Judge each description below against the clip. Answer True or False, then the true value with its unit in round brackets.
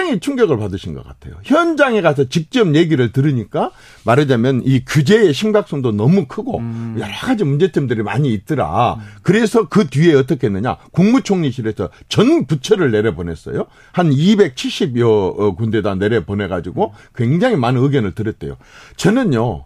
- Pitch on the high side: False (135 Hz)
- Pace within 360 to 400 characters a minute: False (345 characters per minute)